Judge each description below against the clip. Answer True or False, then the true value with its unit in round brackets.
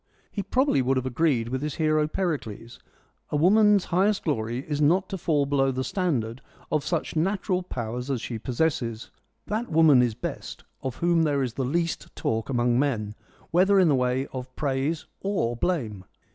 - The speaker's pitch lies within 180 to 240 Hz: False (145 Hz)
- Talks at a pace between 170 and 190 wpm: True (180 wpm)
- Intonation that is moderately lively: False (5.7 semitones)